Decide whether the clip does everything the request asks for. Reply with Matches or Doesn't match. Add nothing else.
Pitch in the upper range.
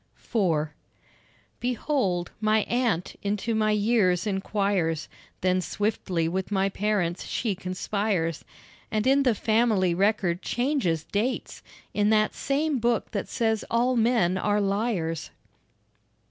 Matches